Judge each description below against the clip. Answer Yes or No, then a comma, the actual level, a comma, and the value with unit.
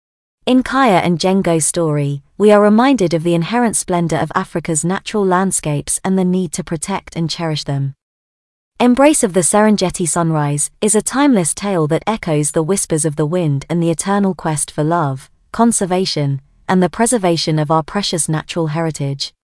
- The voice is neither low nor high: Yes, medium, 175 Hz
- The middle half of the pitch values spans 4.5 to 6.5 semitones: No, average, 3.9 semitones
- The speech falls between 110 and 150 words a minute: No, average, 170 wpm